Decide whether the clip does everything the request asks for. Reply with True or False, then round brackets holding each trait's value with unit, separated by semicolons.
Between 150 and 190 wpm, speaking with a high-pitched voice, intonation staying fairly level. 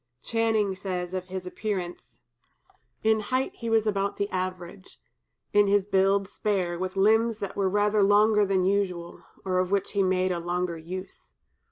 True (165 wpm; 195 Hz; 2.0 semitones)